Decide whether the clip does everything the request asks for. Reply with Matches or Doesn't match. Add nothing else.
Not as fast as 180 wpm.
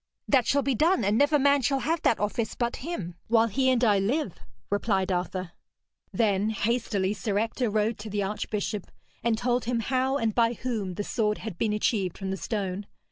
Doesn't match